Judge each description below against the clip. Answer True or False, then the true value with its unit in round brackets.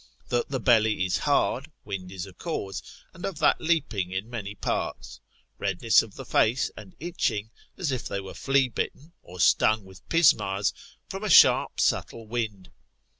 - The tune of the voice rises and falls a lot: True (6.1 semitones)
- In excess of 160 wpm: True (170 wpm)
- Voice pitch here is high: False (110 Hz)